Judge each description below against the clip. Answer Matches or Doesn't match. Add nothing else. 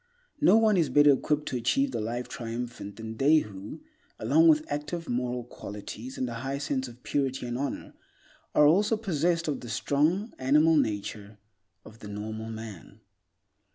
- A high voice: Doesn't match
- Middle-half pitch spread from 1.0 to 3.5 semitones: Doesn't match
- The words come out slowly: Doesn't match